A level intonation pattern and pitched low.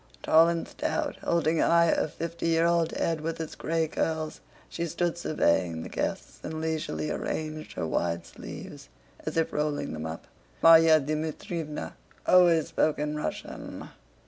No: narrow, 1.6 semitones; medium, 160 Hz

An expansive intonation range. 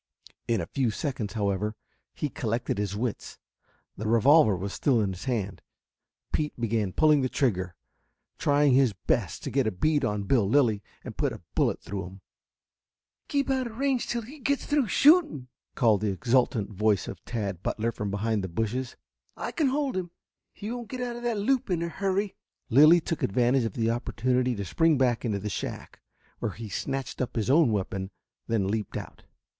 Yes: wide, 7.4 semitones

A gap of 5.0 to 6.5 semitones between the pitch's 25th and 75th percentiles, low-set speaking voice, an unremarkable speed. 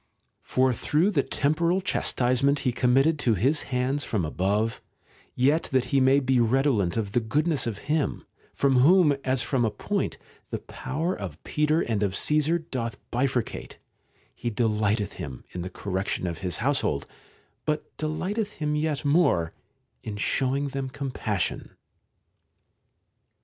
Yes: wide, 5.5 semitones; low, 130 Hz; average, 145 wpm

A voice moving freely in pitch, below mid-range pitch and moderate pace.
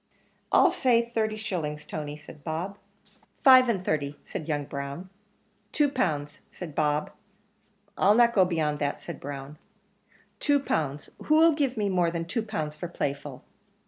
No: wide, 7.0 semitones; medium, 165 Hz; average, 145 wpm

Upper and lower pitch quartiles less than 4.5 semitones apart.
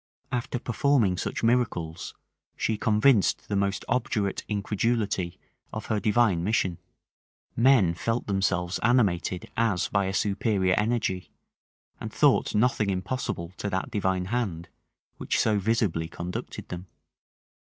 Yes: average, 3.8 semitones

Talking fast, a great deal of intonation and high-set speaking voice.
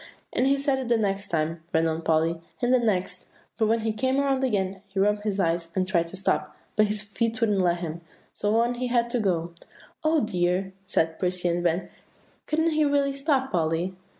Yes: fast, 210 wpm; wide, 5.9 semitones; high, 205 Hz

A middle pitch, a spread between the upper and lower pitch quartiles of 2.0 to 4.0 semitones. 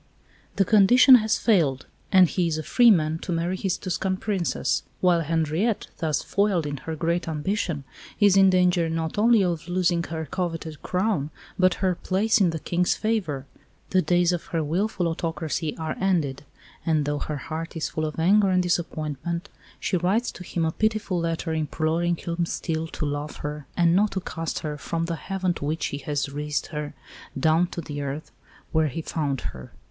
Yes: medium, 170 Hz; average, 3.1 semitones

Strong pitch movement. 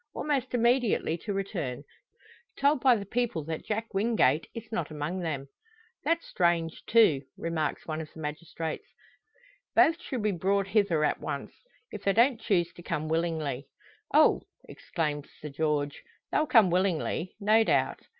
Yes: wide, 6.1 semitones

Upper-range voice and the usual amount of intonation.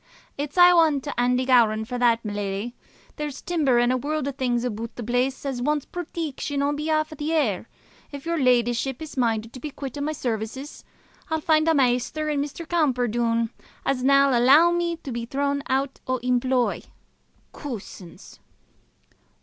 Yes: very high, 265 Hz; average, 3.7 semitones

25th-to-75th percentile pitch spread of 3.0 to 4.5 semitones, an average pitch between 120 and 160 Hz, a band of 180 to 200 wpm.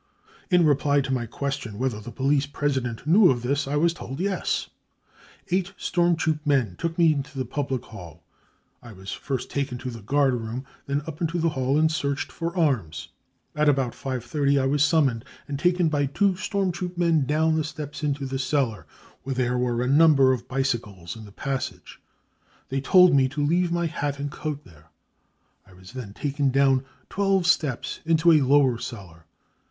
Yes: average, 3.8 semitones; medium, 140 Hz; average, 190 wpm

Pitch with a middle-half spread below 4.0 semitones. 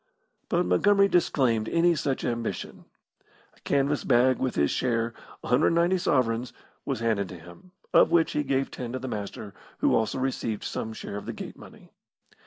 No: average, 4.3 semitones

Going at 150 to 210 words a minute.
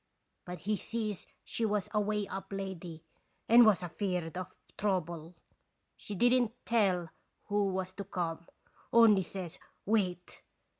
No: slow, 135 wpm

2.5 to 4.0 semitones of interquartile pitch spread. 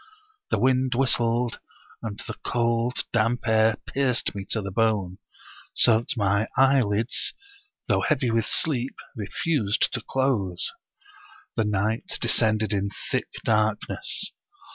Yes: average, 2.9 semitones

